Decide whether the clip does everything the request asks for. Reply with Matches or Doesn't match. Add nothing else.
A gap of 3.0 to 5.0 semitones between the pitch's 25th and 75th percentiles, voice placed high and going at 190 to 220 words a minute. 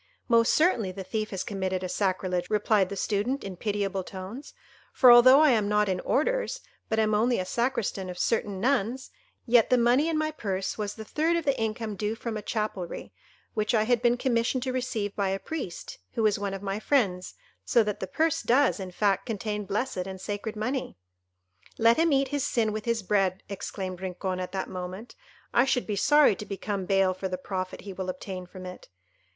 Matches